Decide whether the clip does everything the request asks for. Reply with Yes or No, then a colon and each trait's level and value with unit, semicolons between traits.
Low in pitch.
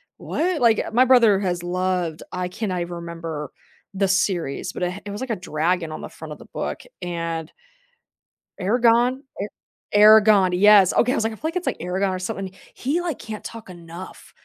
No: high, 190 Hz